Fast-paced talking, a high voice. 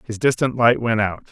No: fast, 230 wpm; low, 115 Hz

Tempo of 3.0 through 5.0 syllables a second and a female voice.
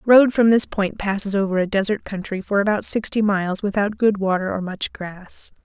No: 5.2 syllables/s; female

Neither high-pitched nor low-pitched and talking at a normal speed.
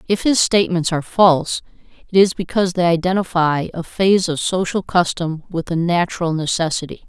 Yes: medium, 175 Hz; average, 160 wpm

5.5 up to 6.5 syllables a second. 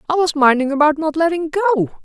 Yes: 5.7 syllables/s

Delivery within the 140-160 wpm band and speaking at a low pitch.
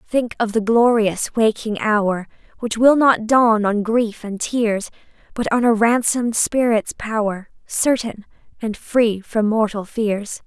No: average, 150 wpm; high, 220 Hz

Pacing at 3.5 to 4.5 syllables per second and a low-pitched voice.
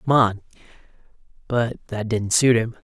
Yes: 4.3 syllables/s; low, 115 Hz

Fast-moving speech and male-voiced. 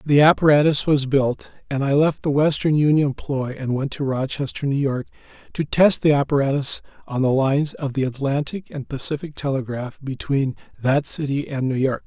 No: average, 180 wpm; male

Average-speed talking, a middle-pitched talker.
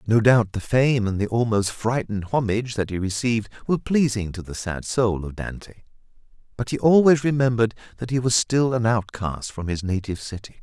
No: average, 190 wpm; low, 110 Hz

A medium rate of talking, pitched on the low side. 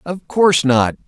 No: average, 165 wpm; medium, 155 Hz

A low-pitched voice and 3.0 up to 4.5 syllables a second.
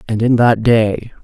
Yes: low, 115 Hz; 4.0 syllables/s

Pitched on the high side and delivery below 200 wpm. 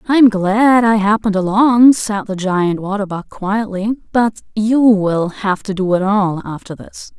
Yes: high, 205 Hz; average, 175 wpm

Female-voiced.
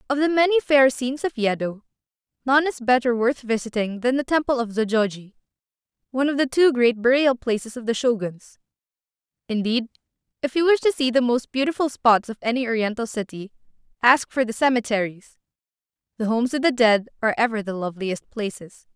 Yes: female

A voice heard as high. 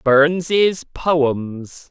No: medium, 150 Hz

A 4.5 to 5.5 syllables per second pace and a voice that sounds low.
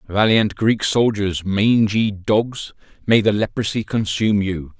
No: 4.0 syllables/s; low, 105 Hz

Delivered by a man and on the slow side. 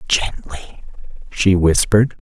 Yes: male; slow, 80 wpm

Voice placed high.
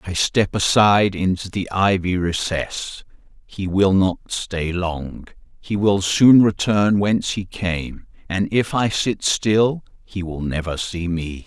No: very low, 95 Hz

